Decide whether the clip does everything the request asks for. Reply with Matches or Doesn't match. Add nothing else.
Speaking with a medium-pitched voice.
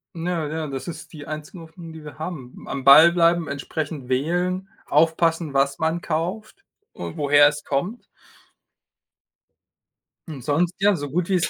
Matches